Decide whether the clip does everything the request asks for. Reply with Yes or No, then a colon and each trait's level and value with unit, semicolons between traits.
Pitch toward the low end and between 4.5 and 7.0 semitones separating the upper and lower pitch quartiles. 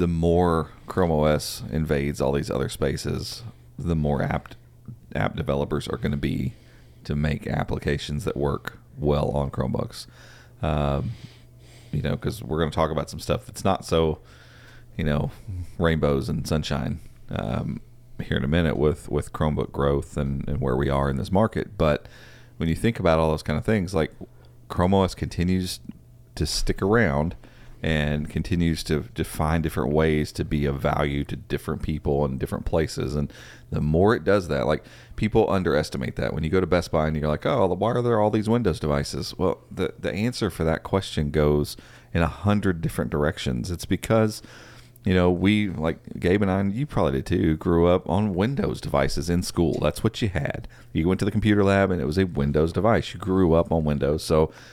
Yes: very low, 80 Hz; average, 5.2 semitones